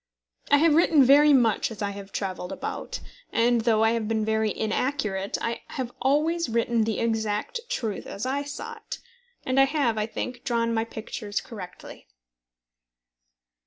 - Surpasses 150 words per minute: Yes, average, 160 wpm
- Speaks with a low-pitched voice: No, high, 230 Hz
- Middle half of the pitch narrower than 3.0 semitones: No, average, 4.1 semitones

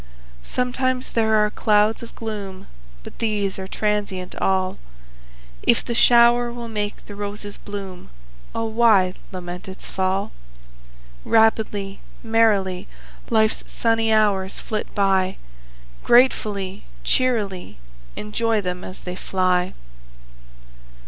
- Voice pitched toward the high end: Yes, high, 210 Hz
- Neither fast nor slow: No, slow, 110 wpm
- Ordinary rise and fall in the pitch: Yes, average, 3.0 semitones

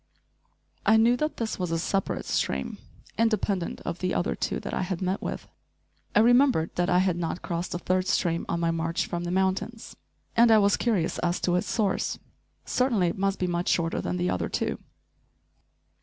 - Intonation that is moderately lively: Yes, average, 3.7 semitones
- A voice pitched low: No, medium, 185 Hz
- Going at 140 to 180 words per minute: No, average, 195 wpm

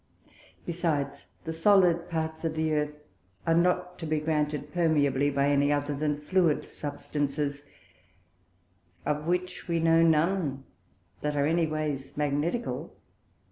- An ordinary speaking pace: No, slow, 130 wpm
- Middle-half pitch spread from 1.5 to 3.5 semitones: Yes, narrow, 2.4 semitones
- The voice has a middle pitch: Yes, medium, 155 Hz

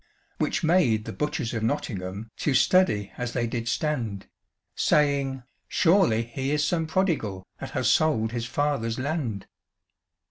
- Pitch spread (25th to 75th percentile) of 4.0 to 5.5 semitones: Yes, average, 5.2 semitones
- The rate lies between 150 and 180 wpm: No, average, 140 wpm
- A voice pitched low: Yes, low, 130 Hz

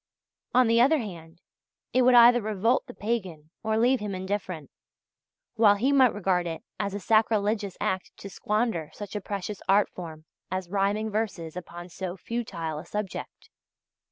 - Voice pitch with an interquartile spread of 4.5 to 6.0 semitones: No, average, 3.8 semitones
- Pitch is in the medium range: No, high, 205 Hz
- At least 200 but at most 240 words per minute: No, average, 160 wpm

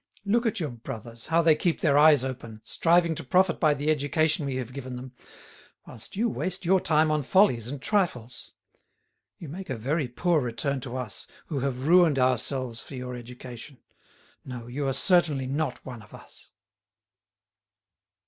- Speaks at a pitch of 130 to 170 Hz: Yes, medium, 140 Hz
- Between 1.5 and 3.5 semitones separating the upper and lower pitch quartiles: No, average, 4.6 semitones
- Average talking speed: Yes, average, 170 wpm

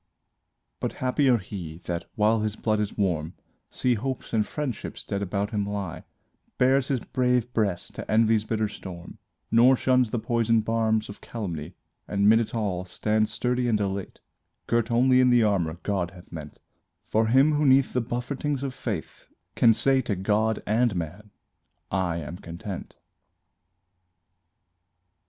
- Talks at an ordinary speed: Yes, average, 155 wpm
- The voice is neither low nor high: No, low, 110 Hz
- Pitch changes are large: No, average, 3.8 semitones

